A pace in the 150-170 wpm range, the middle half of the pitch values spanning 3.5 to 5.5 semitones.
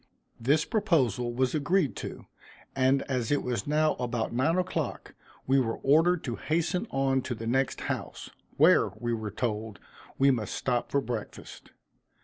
Yes: average, 155 wpm; average, 4.1 semitones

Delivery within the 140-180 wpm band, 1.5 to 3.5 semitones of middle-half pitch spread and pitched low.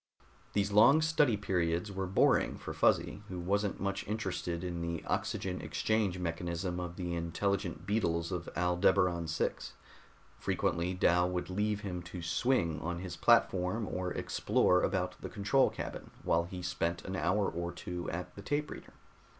Yes: average, 160 wpm; narrow, 2.6 semitones; very low, 90 Hz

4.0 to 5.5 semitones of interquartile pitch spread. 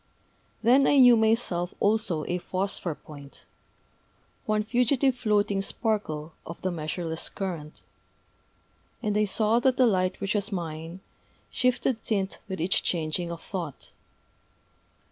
Yes: average, 4.7 semitones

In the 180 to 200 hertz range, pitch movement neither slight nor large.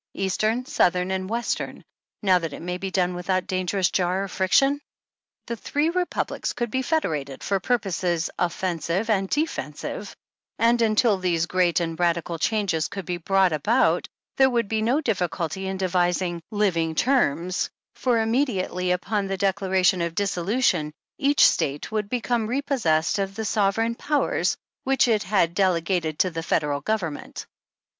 Yes: high, 190 Hz; average, 4.3 semitones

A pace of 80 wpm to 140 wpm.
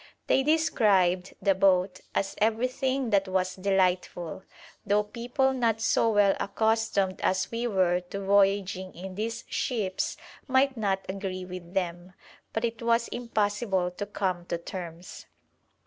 Yes: slow, 135 wpm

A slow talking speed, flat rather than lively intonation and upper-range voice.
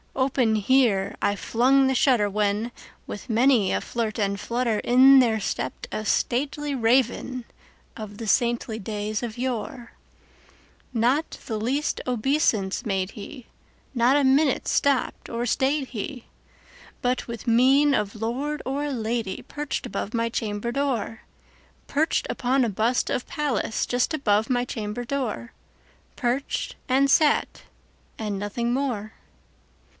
No: slow, 125 wpm; average, 3.6 semitones; high, 240 Hz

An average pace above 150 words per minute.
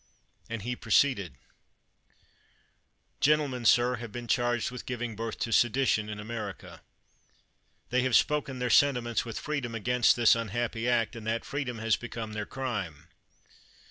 No: average, 145 wpm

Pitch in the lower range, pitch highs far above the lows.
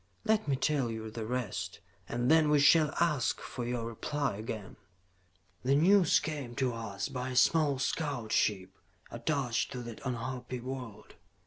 No: low, 125 Hz; average, 4.0 semitones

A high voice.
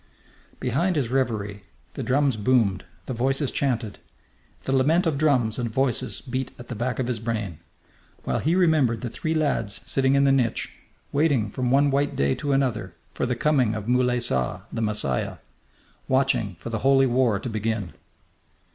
No: low, 125 Hz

